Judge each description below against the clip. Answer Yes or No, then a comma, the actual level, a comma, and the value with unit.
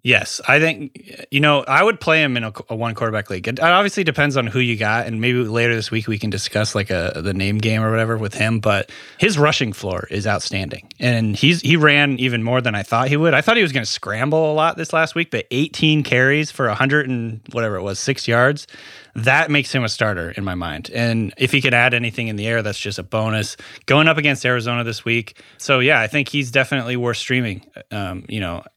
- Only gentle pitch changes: No, average, 4.5 semitones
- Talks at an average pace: No, fast, 245 wpm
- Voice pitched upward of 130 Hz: No, low, 120 Hz